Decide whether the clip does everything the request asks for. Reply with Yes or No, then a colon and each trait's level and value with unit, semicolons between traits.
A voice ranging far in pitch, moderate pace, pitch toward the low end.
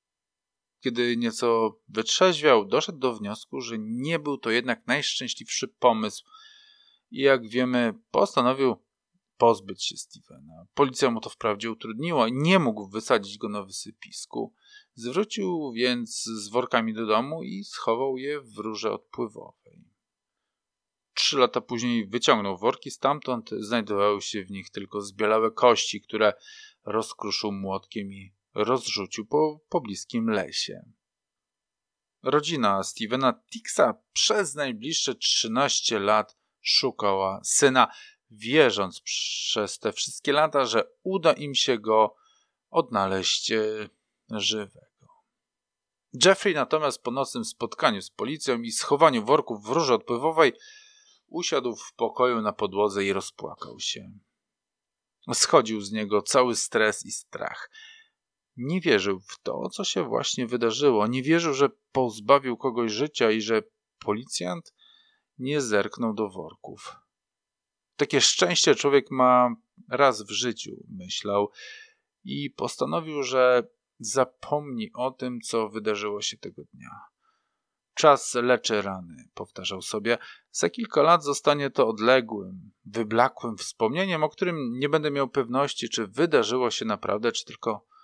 Yes: wide, 6.7 semitones; average, 120 wpm; low, 125 Hz